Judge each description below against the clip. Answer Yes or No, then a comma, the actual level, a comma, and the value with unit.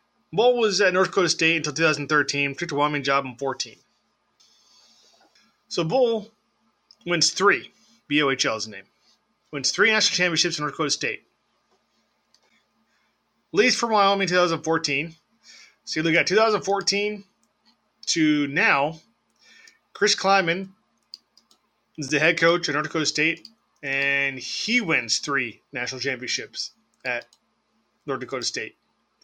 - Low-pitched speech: No, medium, 165 Hz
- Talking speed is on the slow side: Yes, slow, 125 wpm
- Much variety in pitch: Yes, wide, 5.8 semitones